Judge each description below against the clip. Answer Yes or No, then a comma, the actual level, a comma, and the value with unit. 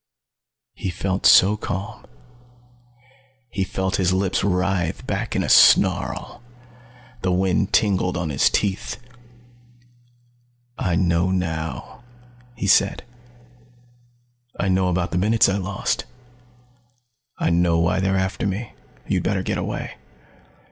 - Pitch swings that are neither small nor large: No, narrow, 1.5 semitones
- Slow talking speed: Yes, slow, 120 wpm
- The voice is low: Yes, very low, 95 Hz